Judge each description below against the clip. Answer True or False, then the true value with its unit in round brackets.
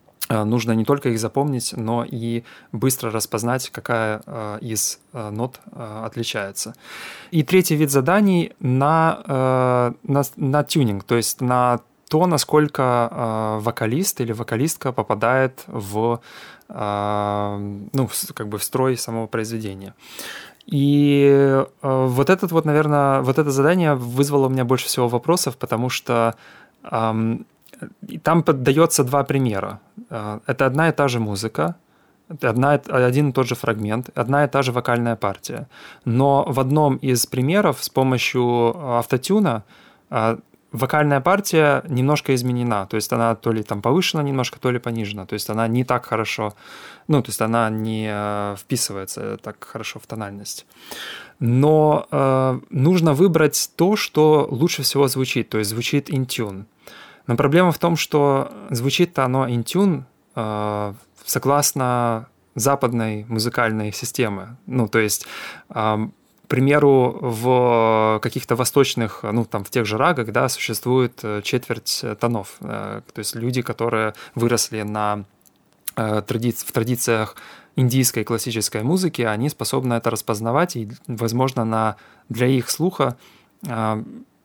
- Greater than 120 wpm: True (130 wpm)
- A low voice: True (125 Hz)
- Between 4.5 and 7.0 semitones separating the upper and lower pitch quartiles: False (3.8 semitones)